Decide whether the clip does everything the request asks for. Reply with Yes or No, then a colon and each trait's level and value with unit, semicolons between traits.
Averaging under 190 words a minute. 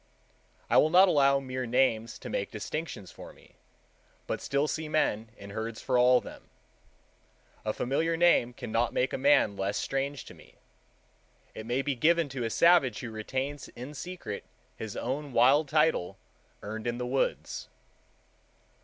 Yes: average, 160 wpm